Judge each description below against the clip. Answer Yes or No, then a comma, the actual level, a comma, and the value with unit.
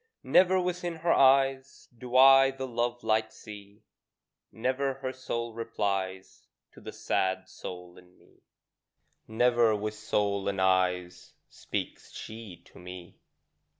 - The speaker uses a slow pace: Yes, slow, 125 wpm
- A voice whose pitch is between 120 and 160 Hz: No, low, 110 Hz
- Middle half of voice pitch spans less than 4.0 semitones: No, wide, 5.6 semitones